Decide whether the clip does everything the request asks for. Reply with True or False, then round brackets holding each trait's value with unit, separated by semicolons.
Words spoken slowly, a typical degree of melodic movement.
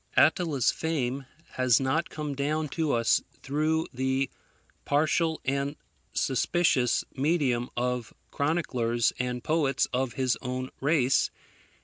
True (110 wpm; 3.6 semitones)